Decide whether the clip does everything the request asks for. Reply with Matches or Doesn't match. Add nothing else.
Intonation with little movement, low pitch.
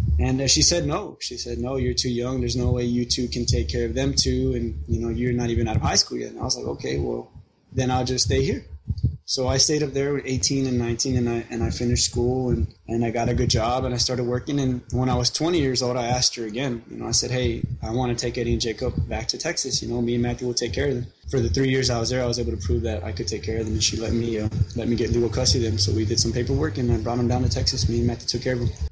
Matches